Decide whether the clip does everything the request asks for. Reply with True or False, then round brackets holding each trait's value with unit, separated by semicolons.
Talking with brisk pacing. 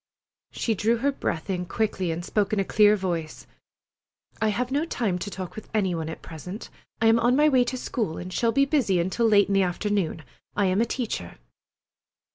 True (210 wpm)